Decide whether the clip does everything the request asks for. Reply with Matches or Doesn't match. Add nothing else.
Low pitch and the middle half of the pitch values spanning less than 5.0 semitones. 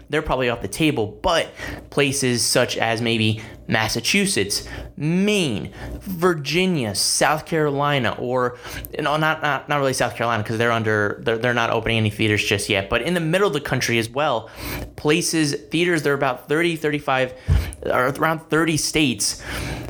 Doesn't match